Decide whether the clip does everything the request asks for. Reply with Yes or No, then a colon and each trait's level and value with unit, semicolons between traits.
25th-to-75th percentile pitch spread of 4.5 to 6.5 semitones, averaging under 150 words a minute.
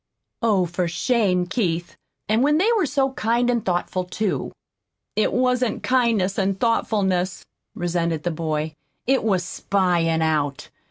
Yes: average, 5.3 semitones; average, 140 wpm